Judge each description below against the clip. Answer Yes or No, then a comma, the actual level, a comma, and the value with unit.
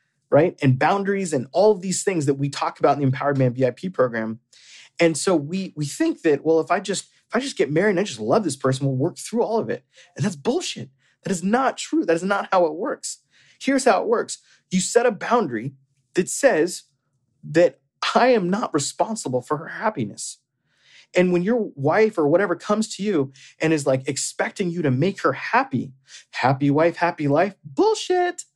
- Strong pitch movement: Yes, wide, 7.4 semitones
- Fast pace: Yes, fast, 210 wpm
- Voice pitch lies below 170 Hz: No, medium, 175 Hz